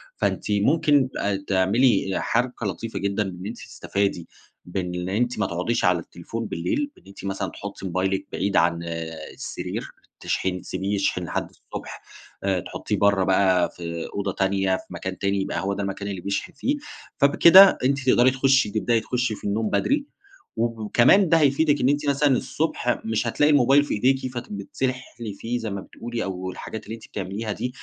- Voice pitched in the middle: No, low, 105 Hz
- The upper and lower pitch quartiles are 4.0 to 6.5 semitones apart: Yes, average, 4.9 semitones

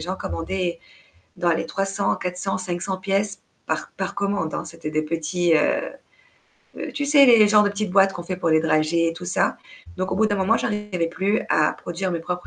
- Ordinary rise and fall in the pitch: Yes, average, 3.1 semitones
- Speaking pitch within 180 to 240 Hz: Yes, medium, 185 Hz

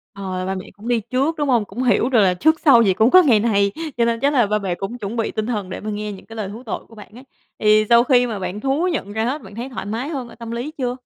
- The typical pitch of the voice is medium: No, high, 230 Hz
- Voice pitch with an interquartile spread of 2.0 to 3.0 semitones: No, average, 3.5 semitones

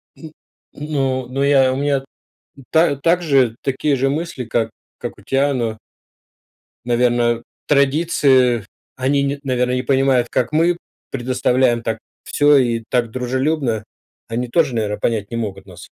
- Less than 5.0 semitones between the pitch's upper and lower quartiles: Yes, average, 2.8 semitones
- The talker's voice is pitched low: Yes, low, 130 Hz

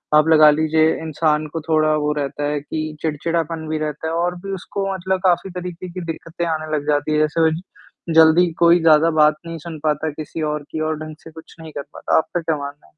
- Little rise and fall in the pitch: Yes, narrow, 1.5 semitones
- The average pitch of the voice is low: No, medium, 160 Hz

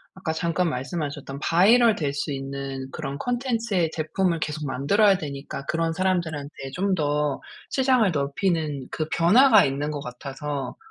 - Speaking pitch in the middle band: Yes, medium, 155 Hz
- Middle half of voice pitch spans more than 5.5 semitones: No, average, 5.1 semitones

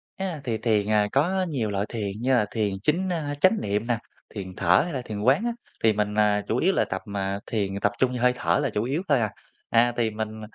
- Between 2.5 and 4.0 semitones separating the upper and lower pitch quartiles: No, average, 5.0 semitones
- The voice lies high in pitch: No, low, 115 Hz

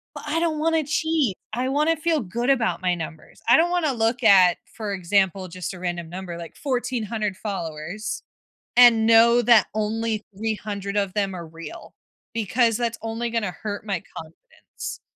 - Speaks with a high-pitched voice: Yes, high, 220 Hz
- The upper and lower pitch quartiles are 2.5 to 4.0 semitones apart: No, average, 4.5 semitones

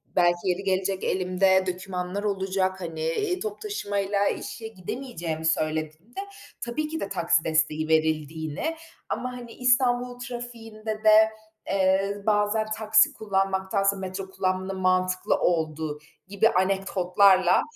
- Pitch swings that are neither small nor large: Yes, average, 3.2 semitones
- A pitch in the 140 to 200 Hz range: Yes, high, 190 Hz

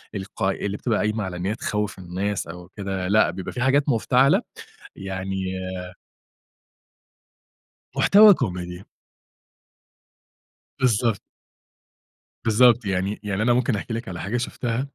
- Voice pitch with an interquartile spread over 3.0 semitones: Yes, average, 4.0 semitones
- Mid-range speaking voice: No, low, 105 Hz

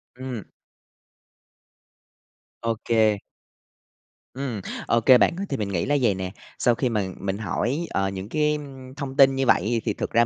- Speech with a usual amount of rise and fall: Yes, average, 4.5 semitones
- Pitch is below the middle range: Yes, low, 120 Hz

